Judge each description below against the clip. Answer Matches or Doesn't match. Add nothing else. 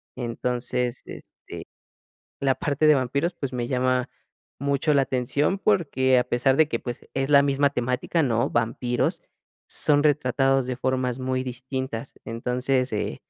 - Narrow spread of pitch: Matches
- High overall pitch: Doesn't match